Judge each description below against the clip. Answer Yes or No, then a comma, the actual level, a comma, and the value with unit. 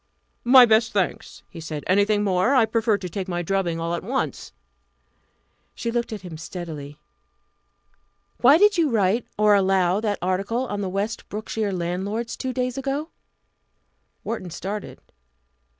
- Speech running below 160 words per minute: Yes, average, 150 wpm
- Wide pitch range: No, average, 4.1 semitones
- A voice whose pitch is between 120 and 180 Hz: No, high, 205 Hz